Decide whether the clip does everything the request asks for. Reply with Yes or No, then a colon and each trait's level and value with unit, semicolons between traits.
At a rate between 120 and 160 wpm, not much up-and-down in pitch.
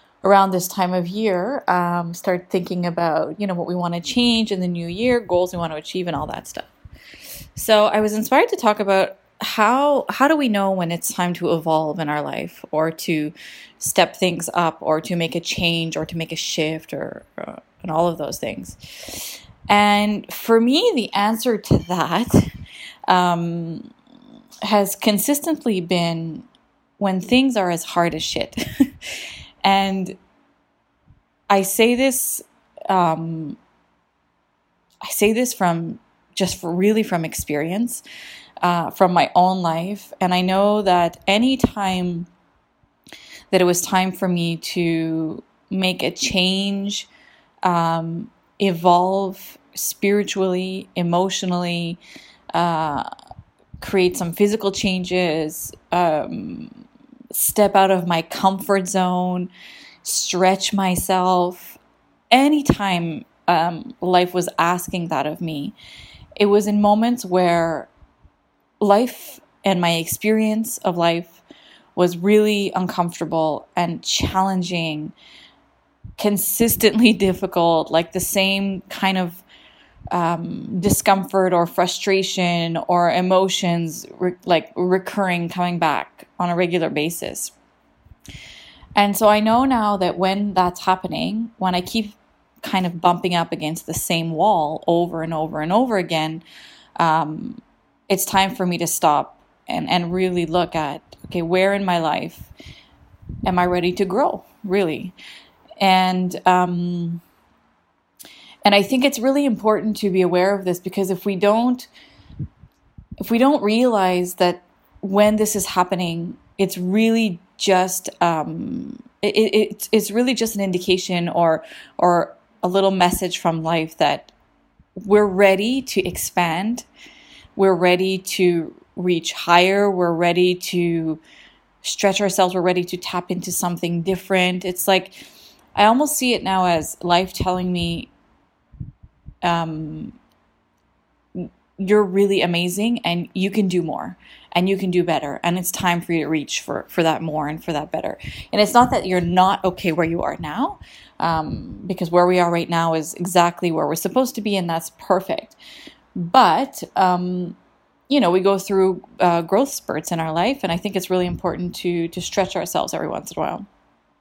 No: average, 145 wpm; average, 3.0 semitones